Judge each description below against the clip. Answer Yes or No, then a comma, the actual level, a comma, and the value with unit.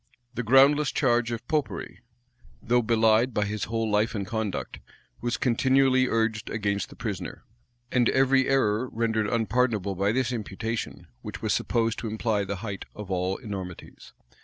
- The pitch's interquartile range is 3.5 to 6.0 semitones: No, average, 2.9 semitones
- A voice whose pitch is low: Yes, low, 115 Hz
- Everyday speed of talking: Yes, average, 155 wpm